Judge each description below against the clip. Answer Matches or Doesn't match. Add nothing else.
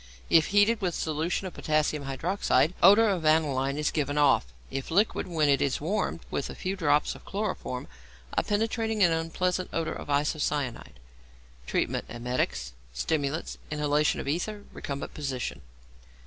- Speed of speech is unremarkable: Matches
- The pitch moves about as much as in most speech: Matches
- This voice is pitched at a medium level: Matches